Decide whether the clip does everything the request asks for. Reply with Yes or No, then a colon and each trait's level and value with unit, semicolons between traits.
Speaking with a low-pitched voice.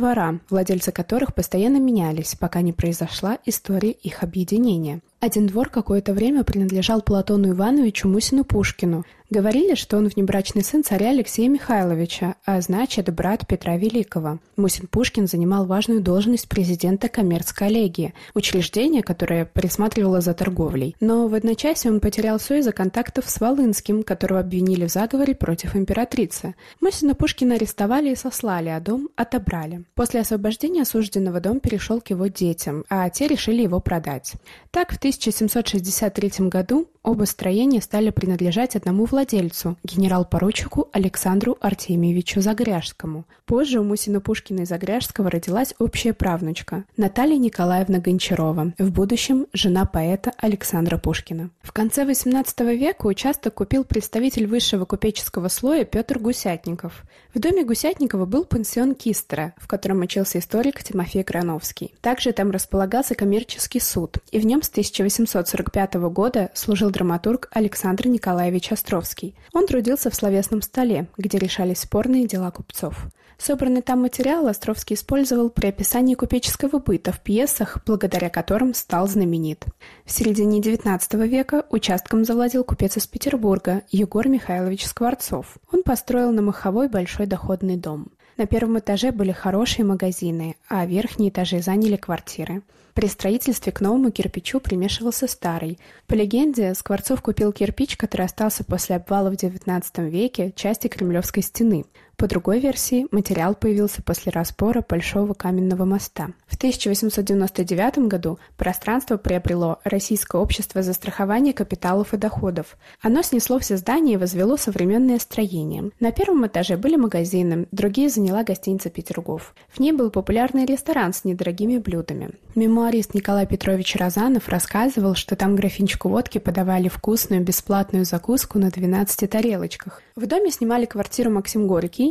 No: high, 205 Hz